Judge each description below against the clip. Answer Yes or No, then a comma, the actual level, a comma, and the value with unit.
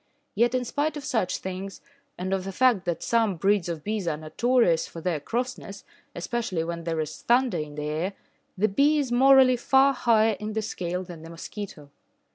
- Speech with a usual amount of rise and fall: No, wide, 6.1 semitones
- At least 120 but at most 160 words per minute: No, average, 195 wpm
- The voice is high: Yes, high, 200 Hz